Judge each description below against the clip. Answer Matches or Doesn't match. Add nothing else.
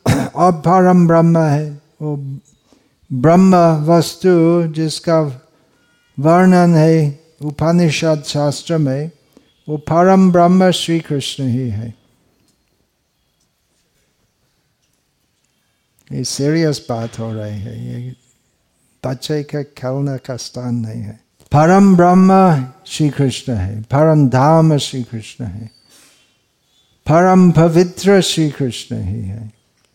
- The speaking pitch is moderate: Matches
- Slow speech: Matches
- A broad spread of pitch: Doesn't match